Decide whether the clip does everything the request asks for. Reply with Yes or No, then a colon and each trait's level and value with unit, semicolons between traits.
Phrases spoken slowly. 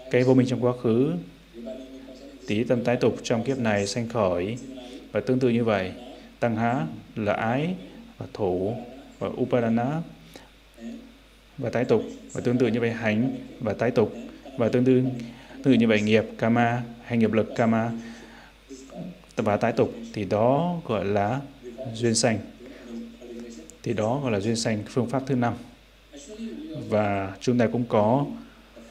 Yes: slow, 160 wpm